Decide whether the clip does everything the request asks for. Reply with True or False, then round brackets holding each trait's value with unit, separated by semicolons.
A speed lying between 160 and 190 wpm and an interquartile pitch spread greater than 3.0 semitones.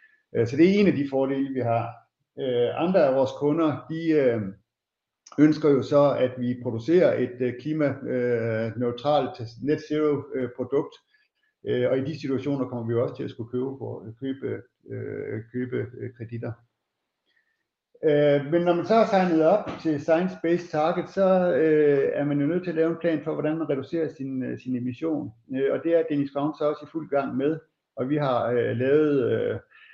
True (165 wpm; 4.2 semitones)